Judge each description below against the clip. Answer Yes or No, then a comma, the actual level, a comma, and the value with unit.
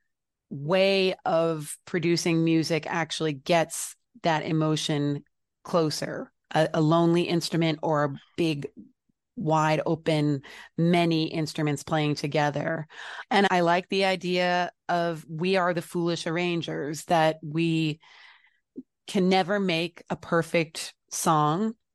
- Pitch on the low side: No, medium, 165 Hz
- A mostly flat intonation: Yes, narrow, 2.2 semitones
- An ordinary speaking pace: No, slow, 110 wpm